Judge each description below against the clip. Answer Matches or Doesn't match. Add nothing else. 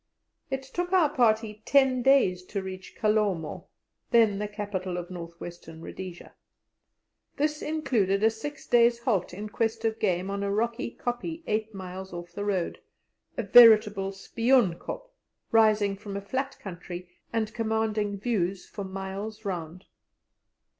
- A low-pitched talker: Doesn't match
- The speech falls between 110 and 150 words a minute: Matches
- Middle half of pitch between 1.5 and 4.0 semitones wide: Matches